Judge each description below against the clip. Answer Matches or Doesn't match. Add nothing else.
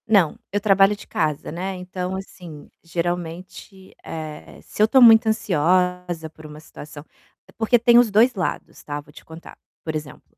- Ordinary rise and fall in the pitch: Matches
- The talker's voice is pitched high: Doesn't match